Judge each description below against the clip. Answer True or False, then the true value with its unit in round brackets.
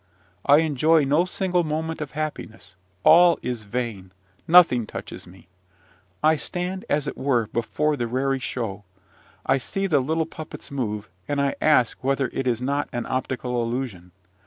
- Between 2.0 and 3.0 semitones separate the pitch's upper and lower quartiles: False (4.6 semitones)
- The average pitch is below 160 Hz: True (135 Hz)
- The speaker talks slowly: False (160 wpm)